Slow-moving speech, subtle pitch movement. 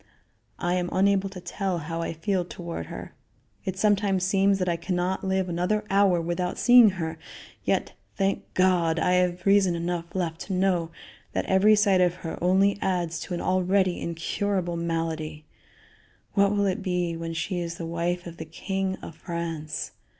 No: average, 175 wpm; narrow, 2.3 semitones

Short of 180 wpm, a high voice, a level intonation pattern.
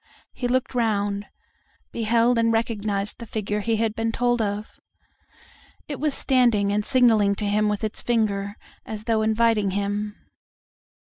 Yes: average, 145 wpm; high, 220 Hz; narrow, 2.2 semitones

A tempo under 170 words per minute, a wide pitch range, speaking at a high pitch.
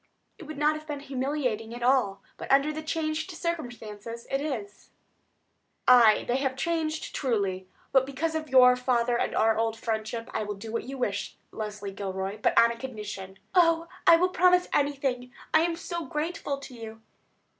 No: average, 175 wpm; wide, 5.7 semitones; very high, 255 Hz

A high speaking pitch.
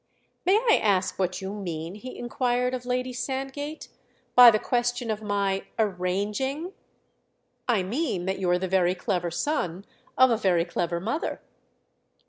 Yes: high, 210 Hz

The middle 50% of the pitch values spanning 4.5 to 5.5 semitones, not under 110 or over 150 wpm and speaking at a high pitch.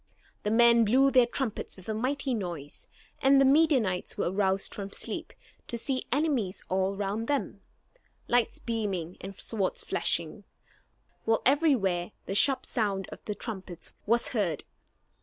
Yes: average, 5.0 semitones; average, 145 wpm; high, 220 Hz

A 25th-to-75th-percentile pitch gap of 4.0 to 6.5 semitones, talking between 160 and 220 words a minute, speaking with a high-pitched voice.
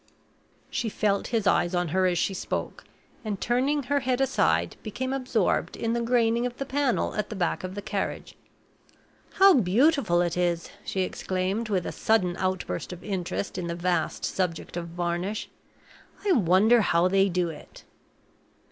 Yes: average, 5.1 semitones; average, 165 wpm; high, 195 Hz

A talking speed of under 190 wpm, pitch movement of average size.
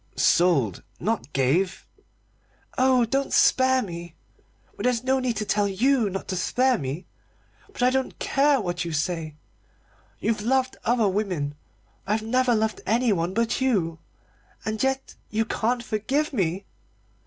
No: average, 145 wpm; wide, 6.0 semitones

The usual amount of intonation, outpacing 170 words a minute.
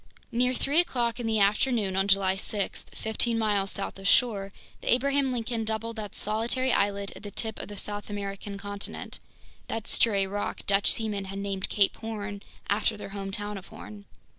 No: narrow, 2.3 semitones; average, 180 wpm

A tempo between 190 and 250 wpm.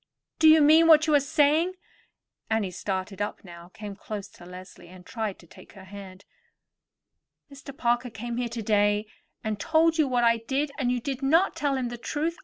Yes: average, 200 wpm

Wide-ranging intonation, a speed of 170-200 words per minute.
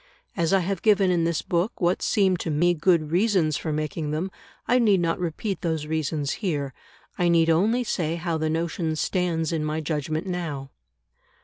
No: average, 2.7 semitones; average, 185 wpm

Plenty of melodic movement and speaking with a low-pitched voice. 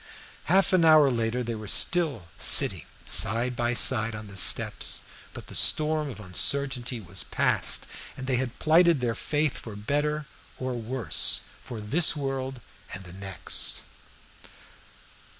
No: average, 4.8 semitones; low, 125 Hz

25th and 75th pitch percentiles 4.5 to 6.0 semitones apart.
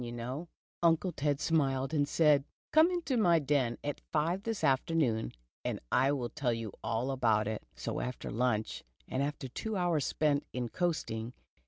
Yes: average, 5.3 semitones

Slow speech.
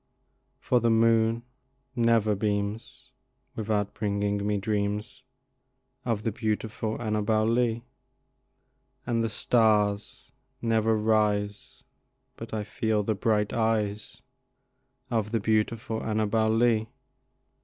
Yes: slow, 100 wpm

